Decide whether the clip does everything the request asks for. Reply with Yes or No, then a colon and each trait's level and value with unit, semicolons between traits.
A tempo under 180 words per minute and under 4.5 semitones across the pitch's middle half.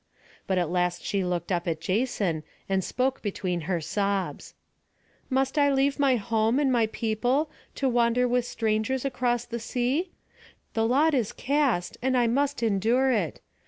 No: average, 160 wpm; average, 5.1 semitones